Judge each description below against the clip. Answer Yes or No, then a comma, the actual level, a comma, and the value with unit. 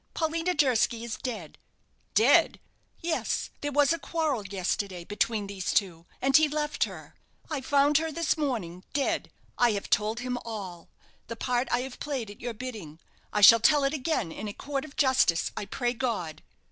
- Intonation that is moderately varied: No, wide, 5.9 semitones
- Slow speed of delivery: No, average, 180 wpm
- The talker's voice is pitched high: Yes, high, 245 Hz